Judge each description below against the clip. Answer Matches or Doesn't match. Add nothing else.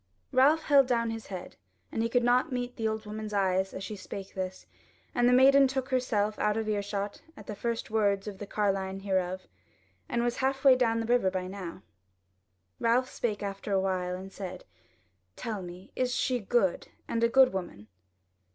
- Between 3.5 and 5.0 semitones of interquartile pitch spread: Matches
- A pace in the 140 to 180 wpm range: Doesn't match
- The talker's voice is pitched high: Matches